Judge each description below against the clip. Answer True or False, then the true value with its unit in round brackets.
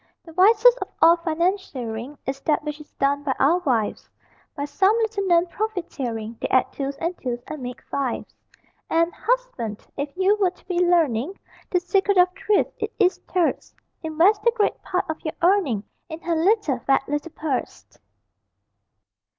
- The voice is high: True (330 Hz)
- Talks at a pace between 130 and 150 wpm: False (165 wpm)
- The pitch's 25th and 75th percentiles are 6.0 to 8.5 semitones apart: False (5.6 semitones)